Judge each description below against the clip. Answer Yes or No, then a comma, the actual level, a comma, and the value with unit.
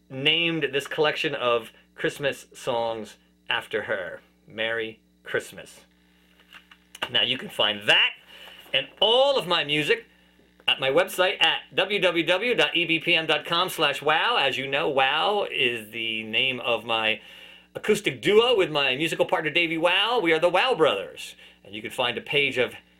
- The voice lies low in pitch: No, medium, 150 Hz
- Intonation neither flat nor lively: No, wide, 7.4 semitones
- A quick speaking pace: No, average, 140 wpm